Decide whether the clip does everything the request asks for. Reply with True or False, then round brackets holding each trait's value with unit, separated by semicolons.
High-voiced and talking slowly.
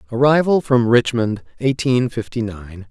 False (120 Hz; 125 wpm)